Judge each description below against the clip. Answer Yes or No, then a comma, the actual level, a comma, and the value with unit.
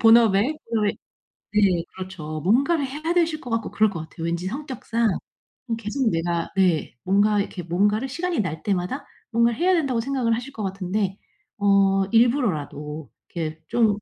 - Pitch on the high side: Yes, high, 210 Hz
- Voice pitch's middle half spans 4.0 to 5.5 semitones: Yes, average, 5.1 semitones